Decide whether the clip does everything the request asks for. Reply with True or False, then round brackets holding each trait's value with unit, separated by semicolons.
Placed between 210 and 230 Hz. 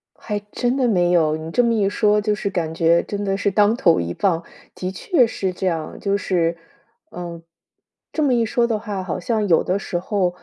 False (195 Hz)